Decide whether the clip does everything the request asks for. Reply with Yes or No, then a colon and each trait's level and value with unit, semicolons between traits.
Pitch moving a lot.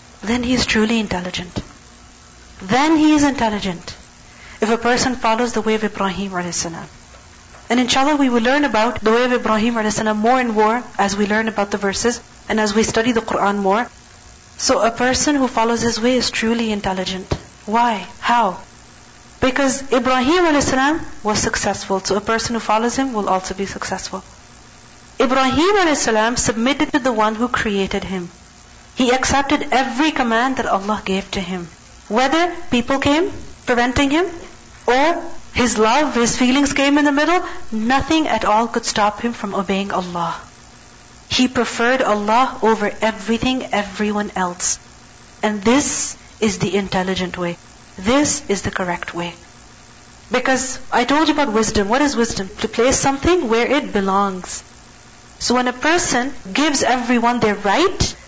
No: average, 4.3 semitones